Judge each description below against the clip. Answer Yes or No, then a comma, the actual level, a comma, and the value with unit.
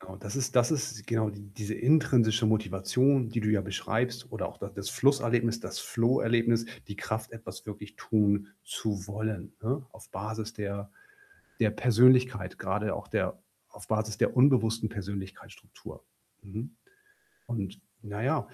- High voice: No, low, 110 Hz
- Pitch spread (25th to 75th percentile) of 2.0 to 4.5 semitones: Yes, average, 2.8 semitones